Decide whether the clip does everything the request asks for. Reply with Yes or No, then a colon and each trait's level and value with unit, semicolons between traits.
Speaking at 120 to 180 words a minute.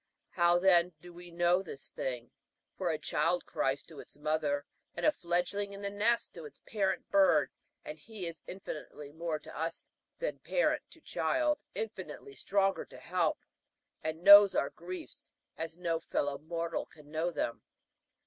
Yes: average, 165 wpm